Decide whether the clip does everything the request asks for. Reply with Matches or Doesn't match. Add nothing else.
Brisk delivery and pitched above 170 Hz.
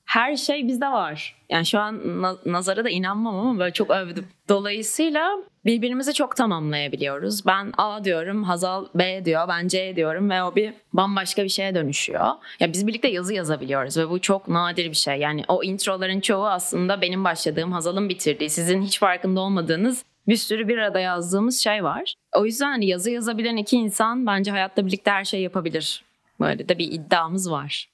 Matches